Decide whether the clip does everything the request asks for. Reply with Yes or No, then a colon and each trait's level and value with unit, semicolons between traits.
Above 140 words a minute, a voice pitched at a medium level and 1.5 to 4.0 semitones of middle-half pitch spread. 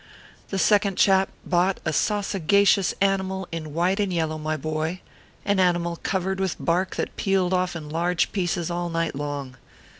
Yes: average, 160 wpm; medium, 180 Hz; average, 2.7 semitones